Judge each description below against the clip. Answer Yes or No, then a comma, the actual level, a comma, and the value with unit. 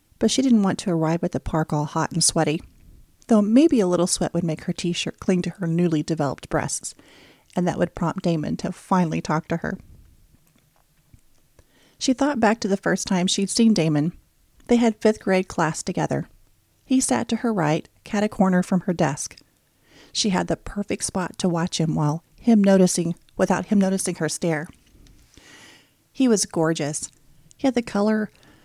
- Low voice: No, medium, 180 Hz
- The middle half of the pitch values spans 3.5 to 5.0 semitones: Yes, average, 4.3 semitones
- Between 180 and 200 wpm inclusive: Yes, average, 185 wpm